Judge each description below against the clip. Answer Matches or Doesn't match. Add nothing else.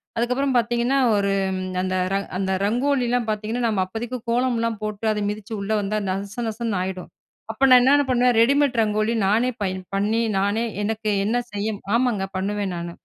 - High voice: Matches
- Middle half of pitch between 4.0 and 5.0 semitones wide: Doesn't match